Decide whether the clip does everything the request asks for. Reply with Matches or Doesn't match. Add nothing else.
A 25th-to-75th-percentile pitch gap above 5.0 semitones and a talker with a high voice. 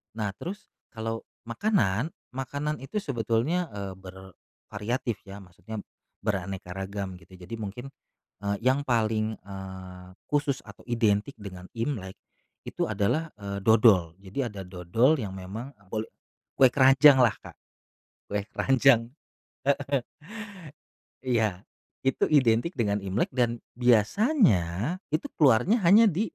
Doesn't match